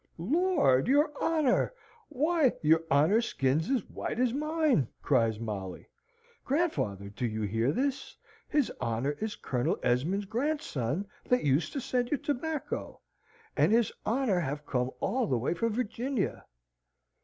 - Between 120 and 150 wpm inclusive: Yes, average, 140 wpm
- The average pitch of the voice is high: Yes, high, 205 Hz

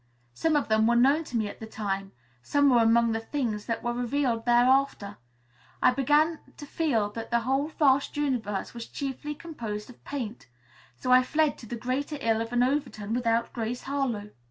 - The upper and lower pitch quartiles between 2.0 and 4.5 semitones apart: Yes, average, 3.8 semitones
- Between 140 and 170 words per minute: No, average, 190 wpm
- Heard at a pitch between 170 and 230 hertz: No, high, 245 Hz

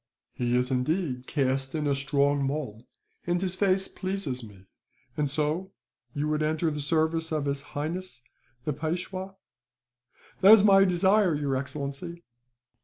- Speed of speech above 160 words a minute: No, average, 145 wpm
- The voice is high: No, medium, 150 Hz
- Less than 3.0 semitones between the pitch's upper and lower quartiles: No, average, 4.6 semitones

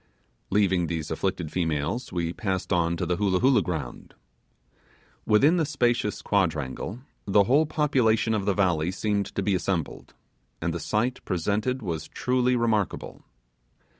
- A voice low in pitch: Yes, low, 100 Hz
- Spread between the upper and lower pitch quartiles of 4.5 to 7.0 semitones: Yes, wide, 5.4 semitones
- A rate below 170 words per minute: Yes, average, 140 wpm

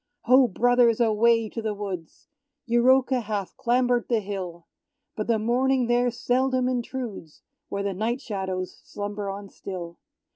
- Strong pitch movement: No, average, 3.6 semitones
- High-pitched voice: Yes, high, 230 Hz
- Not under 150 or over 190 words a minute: No, average, 140 wpm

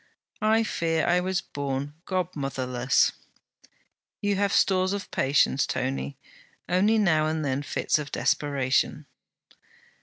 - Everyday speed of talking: No, slow, 115 wpm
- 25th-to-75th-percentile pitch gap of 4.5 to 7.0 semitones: Yes, wide, 5.6 semitones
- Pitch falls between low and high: Yes, medium, 155 Hz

